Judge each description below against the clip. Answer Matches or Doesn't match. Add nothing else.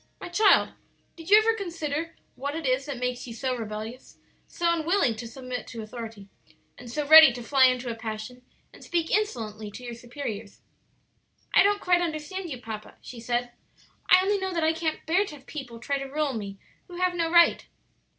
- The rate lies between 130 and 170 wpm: Doesn't match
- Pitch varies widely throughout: Matches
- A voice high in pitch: Matches